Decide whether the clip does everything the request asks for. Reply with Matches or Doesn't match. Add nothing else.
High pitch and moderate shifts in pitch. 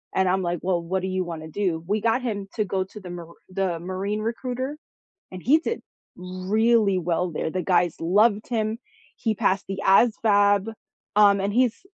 Matches